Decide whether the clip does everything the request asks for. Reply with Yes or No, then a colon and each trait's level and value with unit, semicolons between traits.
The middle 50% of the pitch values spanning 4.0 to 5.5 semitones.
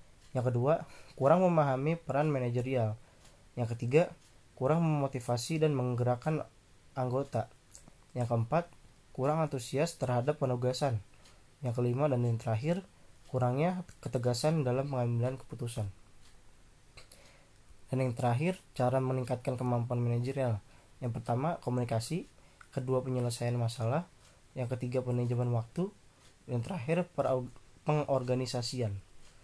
No: average, 2.9 semitones